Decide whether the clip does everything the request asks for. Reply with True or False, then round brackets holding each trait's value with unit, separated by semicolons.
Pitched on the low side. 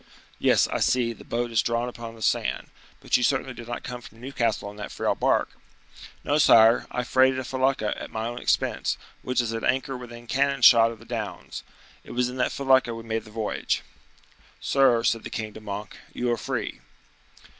True (120 Hz)